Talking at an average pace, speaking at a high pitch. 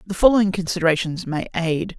No: average, 150 wpm; medium, 175 Hz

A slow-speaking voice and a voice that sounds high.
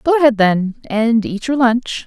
No: fast, 205 wpm; high, 235 Hz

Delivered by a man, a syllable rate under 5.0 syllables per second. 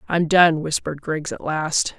No: female; 4.4 syllables/s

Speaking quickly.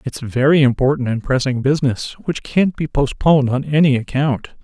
No: average, 170 wpm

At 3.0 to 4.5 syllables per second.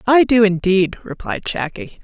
Yes: 4.4 syllables/s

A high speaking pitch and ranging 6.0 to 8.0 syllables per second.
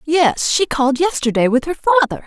Yes: very high, 305 Hz; 6.2 syllables/s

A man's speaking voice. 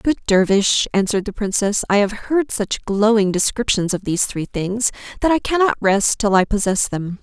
No: female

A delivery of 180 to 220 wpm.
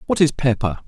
Yes: fast, 205 wpm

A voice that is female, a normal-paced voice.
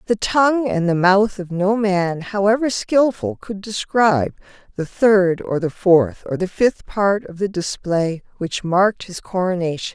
Yes: female; average, 170 wpm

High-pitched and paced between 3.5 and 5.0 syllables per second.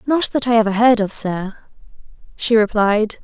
Yes: high, 220 Hz; 4.6 syllables/s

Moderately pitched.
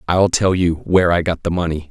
No: very low, 85 Hz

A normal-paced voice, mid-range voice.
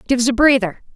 No: average, 190 wpm; high, 245 Hz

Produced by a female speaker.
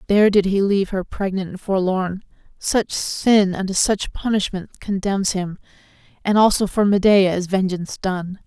Yes: female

